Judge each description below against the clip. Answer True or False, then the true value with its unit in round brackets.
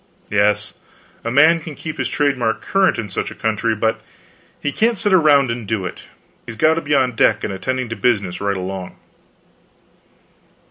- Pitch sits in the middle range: False (115 Hz)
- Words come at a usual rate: True (185 wpm)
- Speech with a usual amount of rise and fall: False (6.0 semitones)